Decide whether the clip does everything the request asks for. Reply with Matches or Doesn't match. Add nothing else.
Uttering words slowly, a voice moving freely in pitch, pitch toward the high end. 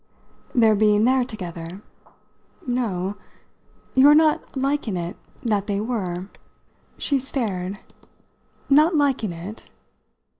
Matches